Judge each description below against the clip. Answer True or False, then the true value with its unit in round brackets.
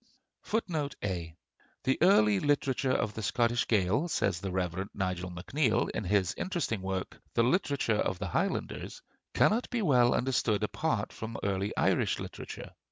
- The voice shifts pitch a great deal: True (5.7 semitones)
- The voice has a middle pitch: False (110 Hz)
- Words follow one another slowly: False (145 wpm)